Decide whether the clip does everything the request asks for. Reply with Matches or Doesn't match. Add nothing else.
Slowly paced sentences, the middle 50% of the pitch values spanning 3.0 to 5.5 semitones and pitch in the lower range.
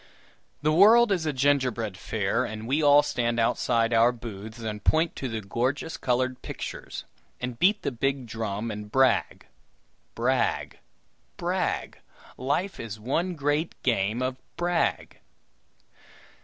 Matches